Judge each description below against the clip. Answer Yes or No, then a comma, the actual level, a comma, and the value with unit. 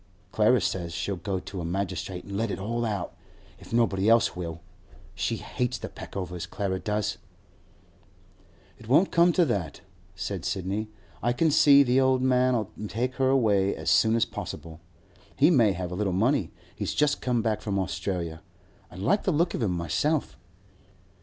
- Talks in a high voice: No, low, 105 Hz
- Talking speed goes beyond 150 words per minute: Yes, average, 170 wpm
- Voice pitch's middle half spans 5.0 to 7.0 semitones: Yes, wide, 5.5 semitones